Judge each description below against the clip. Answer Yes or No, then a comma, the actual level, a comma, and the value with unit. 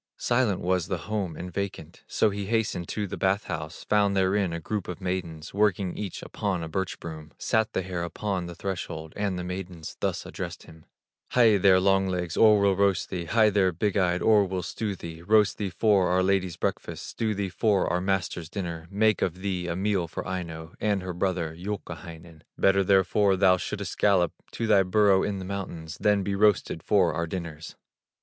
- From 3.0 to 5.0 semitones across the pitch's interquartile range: No, narrow, 2.6 semitones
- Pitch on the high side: No, very low, 95 Hz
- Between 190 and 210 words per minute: Yes, average, 200 wpm